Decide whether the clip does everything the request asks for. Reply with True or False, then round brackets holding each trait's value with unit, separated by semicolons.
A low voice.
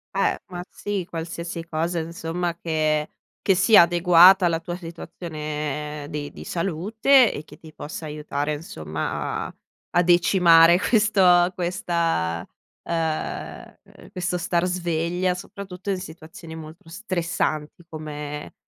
False (170 Hz)